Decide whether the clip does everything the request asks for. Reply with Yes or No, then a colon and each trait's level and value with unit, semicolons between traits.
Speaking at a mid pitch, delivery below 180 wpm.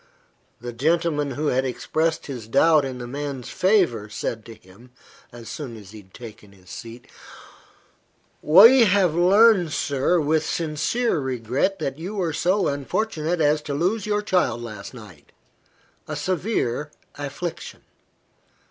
Yes: medium, 145 Hz; average, 140 wpm